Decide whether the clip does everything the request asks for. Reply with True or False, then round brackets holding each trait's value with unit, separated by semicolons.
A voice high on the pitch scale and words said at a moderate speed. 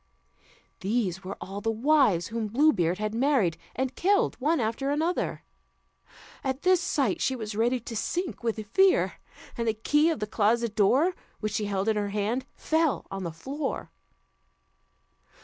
True (230 Hz; 165 wpm)